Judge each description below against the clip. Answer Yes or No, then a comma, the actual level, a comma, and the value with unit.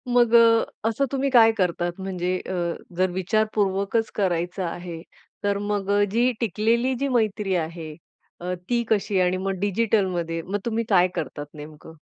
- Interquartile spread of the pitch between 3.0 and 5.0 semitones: Yes, average, 4.1 semitones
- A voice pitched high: Yes, high, 195 Hz